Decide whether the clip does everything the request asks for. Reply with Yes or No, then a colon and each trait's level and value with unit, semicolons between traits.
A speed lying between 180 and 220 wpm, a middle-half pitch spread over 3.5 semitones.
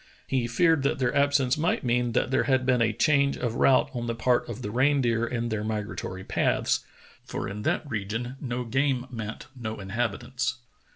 No: average, 185 wpm; average, 2.9 semitones